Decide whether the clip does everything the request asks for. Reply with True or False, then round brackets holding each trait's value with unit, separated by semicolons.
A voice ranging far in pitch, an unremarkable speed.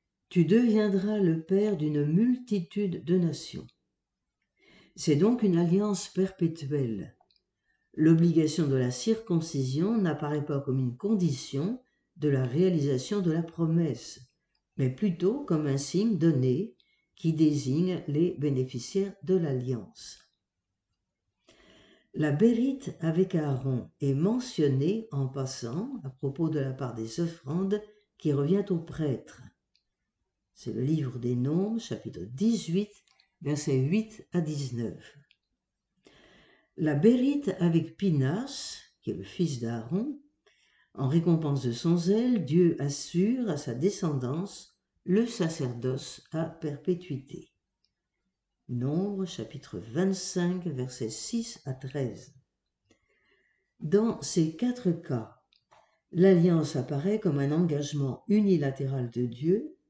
False (5.8 semitones; 110 wpm)